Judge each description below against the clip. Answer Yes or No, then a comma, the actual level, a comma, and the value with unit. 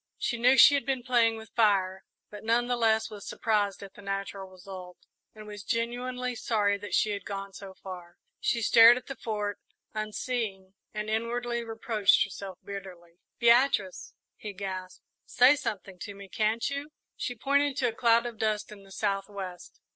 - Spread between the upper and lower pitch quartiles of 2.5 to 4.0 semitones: Yes, average, 3.2 semitones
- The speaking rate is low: No, average, 175 wpm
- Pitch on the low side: No, high, 215 Hz